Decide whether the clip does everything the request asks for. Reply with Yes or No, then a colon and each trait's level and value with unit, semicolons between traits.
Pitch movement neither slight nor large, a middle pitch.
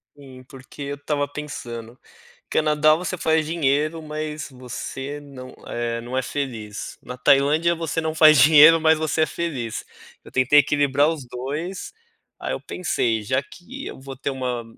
Yes: average, 3.4 semitones; medium, 145 Hz